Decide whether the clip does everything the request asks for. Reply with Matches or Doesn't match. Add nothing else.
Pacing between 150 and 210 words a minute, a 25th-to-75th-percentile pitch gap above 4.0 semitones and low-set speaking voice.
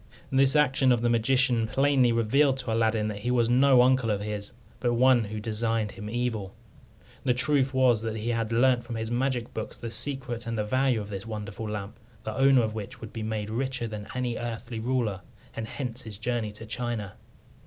Doesn't match